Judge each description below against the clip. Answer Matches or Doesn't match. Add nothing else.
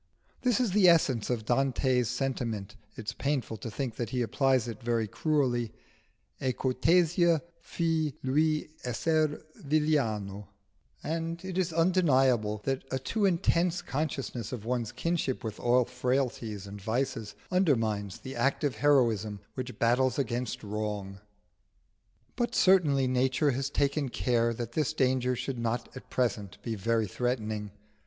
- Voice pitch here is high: Doesn't match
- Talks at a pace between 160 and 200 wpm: Doesn't match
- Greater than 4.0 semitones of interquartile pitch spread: Matches